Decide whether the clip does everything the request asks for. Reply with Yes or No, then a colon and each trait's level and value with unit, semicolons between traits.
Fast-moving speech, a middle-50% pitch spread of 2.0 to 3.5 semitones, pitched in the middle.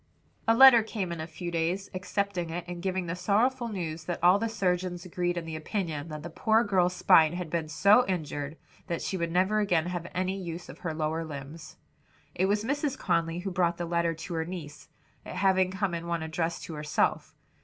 Yes: fast, 210 wpm; average, 2.7 semitones; medium, 175 Hz